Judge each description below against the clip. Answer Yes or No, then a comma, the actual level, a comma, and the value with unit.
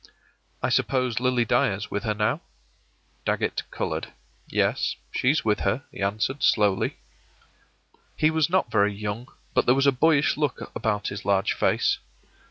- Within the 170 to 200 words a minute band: No, average, 155 wpm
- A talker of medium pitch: No, low, 115 Hz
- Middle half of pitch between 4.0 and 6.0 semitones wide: Yes, average, 4.9 semitones